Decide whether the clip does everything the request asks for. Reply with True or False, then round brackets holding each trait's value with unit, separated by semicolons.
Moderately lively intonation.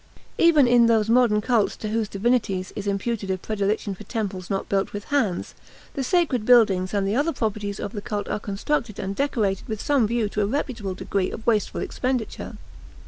True (3.4 semitones)